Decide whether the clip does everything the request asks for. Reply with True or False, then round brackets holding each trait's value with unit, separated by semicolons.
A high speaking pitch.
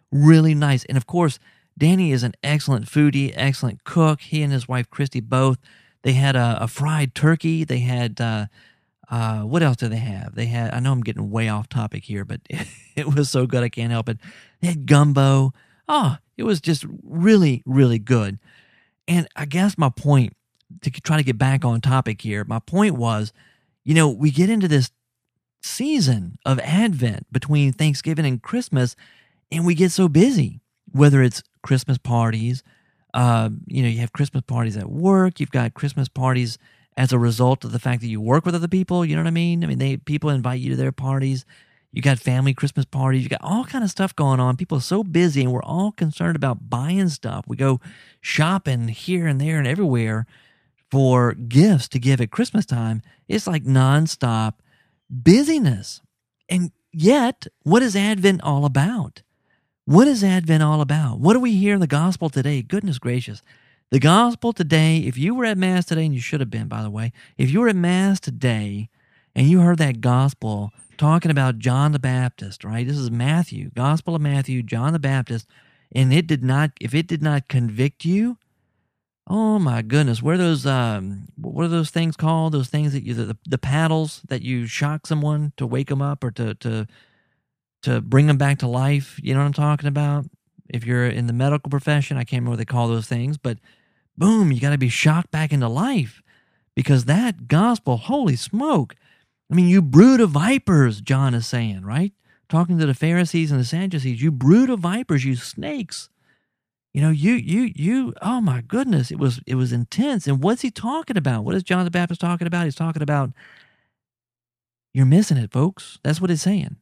False (140 Hz)